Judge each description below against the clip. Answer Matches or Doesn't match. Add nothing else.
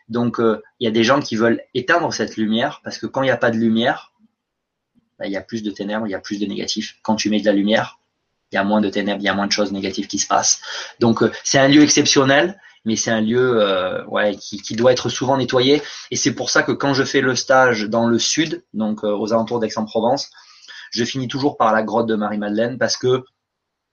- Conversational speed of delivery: Doesn't match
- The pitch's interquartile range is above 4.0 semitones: Doesn't match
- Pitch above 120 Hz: Doesn't match